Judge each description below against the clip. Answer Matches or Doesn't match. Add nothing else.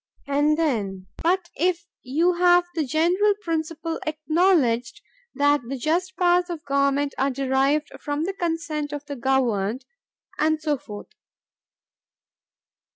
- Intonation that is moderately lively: Matches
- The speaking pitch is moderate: Doesn't match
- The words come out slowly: Matches